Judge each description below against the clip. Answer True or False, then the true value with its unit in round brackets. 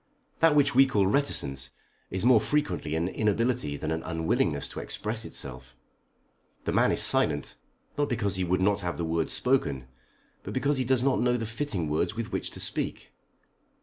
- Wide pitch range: True (7.7 semitones)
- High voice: False (105 Hz)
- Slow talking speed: False (180 wpm)